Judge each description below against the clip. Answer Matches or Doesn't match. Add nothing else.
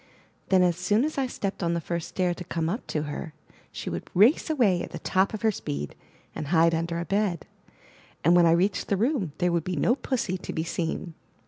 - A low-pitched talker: Doesn't match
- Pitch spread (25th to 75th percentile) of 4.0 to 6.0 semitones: Doesn't match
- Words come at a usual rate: Doesn't match